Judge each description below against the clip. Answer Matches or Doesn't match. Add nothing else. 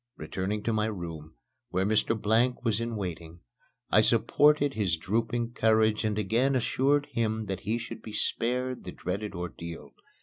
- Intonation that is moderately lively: Matches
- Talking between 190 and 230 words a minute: Doesn't match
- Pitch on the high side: Doesn't match